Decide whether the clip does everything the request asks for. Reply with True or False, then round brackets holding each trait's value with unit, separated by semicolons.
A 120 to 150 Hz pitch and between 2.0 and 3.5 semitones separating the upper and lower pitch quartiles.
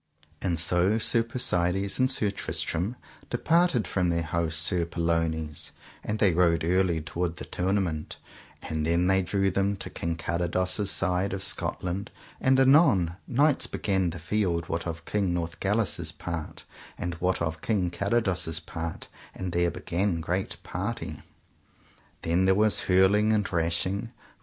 False (90 Hz; 3.1 semitones)